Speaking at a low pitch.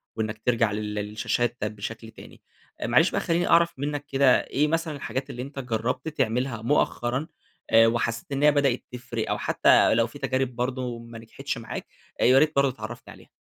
Yes: low, 125 Hz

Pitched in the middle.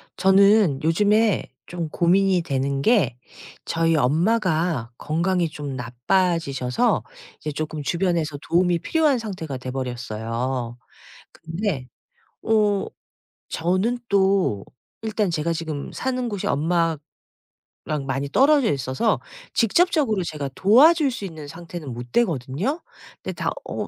Yes: medium, 170 Hz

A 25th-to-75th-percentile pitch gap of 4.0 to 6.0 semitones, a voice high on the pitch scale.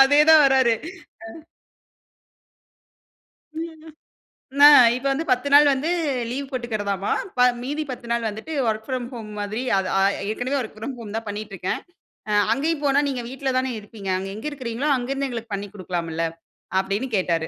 Yes: average, 4.6 semitones; high, 245 Hz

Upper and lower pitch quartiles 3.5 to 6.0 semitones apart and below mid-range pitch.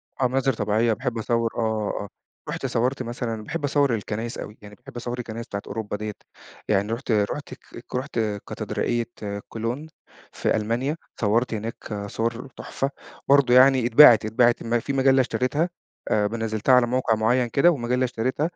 No: average, 2.7 semitones; low, 120 Hz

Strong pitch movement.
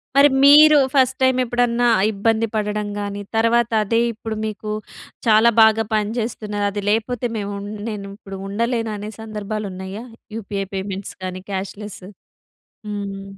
No: narrow, 2.4 semitones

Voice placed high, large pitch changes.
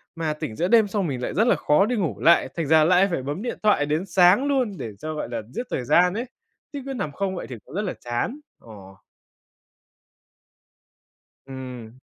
No: medium, 170 Hz; wide, 6.6 semitones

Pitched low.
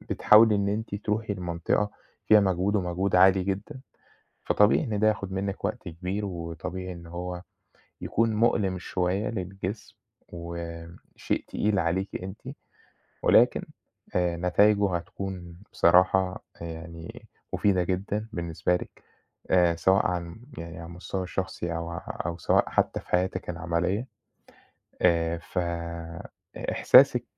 Yes: very low, 90 Hz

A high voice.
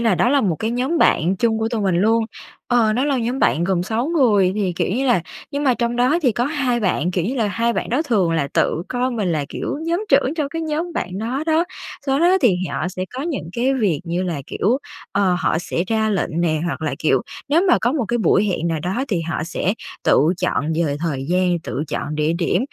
Yes: high, 220 Hz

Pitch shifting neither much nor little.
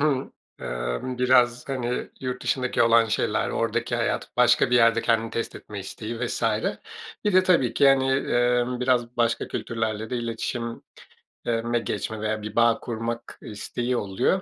No: narrow, 1.7 semitones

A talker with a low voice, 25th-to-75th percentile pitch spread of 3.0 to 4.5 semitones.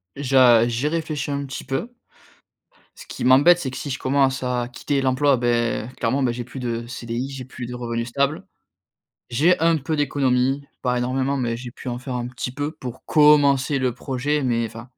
No: low, 130 Hz; narrow, 2.6 semitones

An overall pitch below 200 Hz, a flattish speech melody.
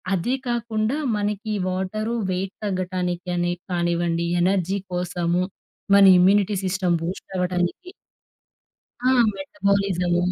Yes: medium, 185 Hz; narrow, 2.2 semitones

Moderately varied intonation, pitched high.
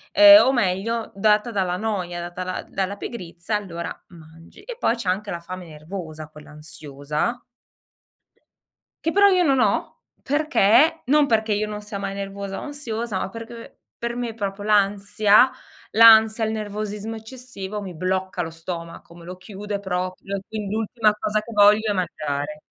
Yes: average, 3.6 semitones; high, 205 Hz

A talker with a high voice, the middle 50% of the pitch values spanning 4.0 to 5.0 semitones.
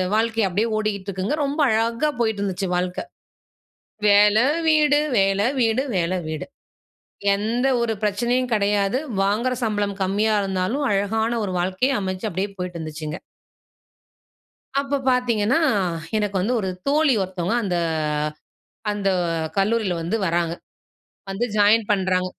No: high, 205 Hz; average, 3.6 semitones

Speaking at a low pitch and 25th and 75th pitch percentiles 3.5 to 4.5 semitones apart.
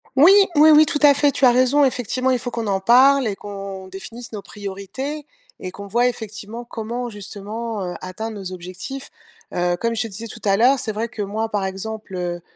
No: high, 220 Hz; average, 4.1 semitones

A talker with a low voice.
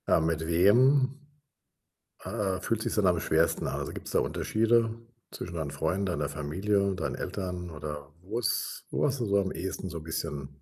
Yes: very low, 95 Hz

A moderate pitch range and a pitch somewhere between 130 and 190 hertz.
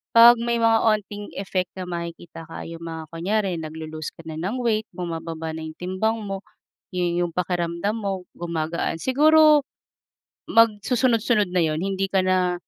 Yes: average, 4.7 semitones; medium, 185 Hz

